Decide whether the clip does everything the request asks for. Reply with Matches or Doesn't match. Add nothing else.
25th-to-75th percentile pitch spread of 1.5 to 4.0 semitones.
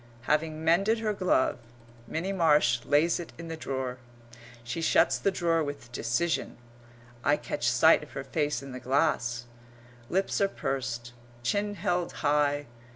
Doesn't match